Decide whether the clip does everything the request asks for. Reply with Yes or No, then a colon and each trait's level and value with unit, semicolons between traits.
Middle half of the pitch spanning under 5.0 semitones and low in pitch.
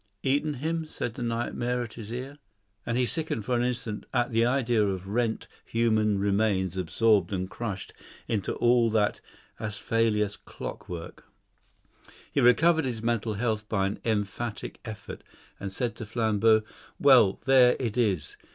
Yes: average, 2.9 semitones; low, 115 Hz